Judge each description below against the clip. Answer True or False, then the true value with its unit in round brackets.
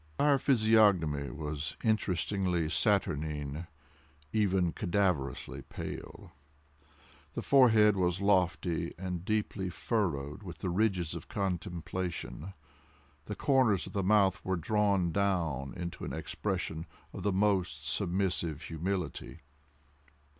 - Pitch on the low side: True (90 Hz)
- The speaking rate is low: True (105 wpm)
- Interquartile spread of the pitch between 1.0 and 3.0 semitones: False (4.0 semitones)